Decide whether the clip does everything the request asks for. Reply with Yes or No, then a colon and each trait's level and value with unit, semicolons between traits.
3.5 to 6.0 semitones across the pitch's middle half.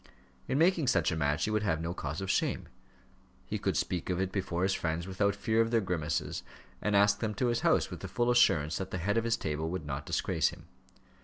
Yes: average, 5.2 semitones